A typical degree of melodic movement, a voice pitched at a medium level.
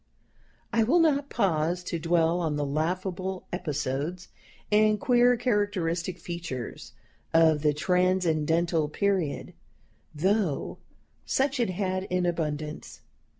Yes: average, 4.1 semitones; medium, 180 Hz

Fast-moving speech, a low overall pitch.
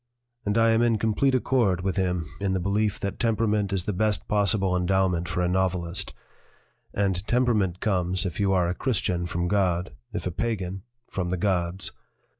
No: average, 180 wpm; very low, 95 Hz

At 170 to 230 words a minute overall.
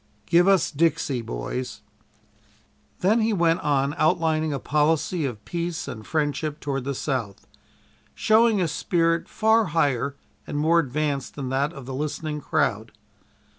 No: average, 140 wpm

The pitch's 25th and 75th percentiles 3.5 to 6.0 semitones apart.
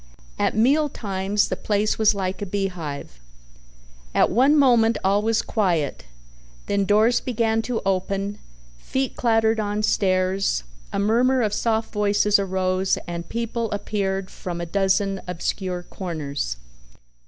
No: average, 3.1 semitones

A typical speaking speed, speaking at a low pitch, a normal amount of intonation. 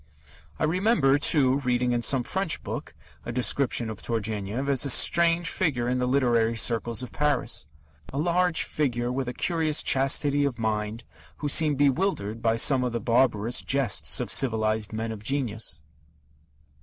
Yes: average, 160 wpm; low, 125 Hz; average, 4.0 semitones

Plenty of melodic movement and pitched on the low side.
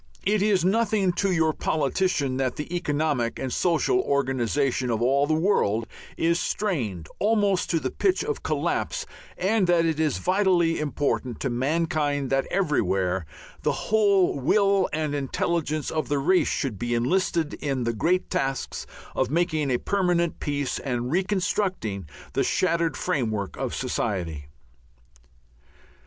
No: wide, 5.9 semitones; medium, 155 Hz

